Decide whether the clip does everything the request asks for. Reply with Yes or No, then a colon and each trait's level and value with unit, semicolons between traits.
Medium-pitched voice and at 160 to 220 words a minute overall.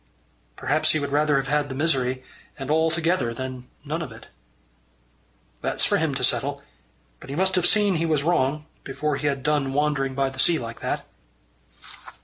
Yes: medium, 145 Hz; average, 185 wpm